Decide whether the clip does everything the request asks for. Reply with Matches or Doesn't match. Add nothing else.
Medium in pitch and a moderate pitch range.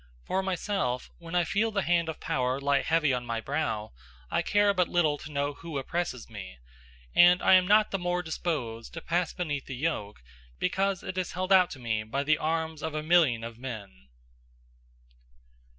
Doesn't match